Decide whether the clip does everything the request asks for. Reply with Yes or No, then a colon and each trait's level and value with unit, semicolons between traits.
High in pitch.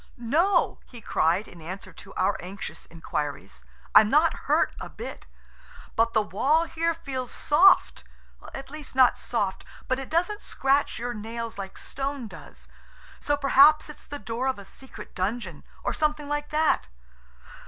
Yes: very high, 250 Hz